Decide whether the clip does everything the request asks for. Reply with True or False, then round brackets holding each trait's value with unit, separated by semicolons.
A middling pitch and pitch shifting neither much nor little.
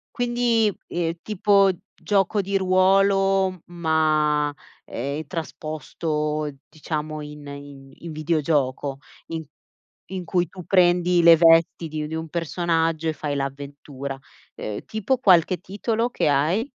True (165 Hz; 4.0 semitones)